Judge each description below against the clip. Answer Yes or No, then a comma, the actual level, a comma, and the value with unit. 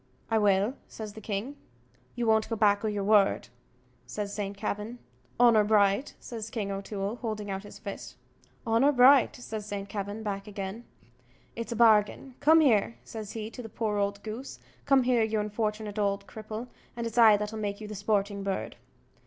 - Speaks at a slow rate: No, average, 180 wpm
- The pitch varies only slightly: Yes, narrow, 2.0 semitones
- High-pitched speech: Yes, high, 215 Hz